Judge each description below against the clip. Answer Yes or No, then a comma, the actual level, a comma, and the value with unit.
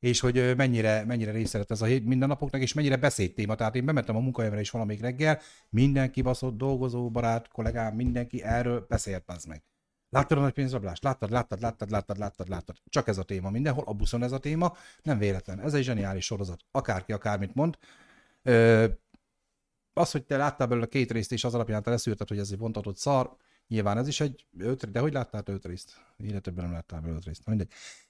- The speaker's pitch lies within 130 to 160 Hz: No, low, 115 Hz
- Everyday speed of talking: No, fast, 205 wpm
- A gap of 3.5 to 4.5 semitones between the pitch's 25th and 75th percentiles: Yes, average, 4.0 semitones